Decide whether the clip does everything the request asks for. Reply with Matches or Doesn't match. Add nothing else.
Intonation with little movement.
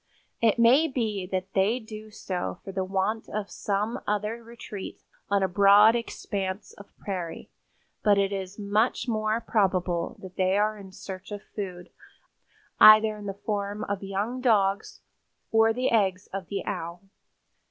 Matches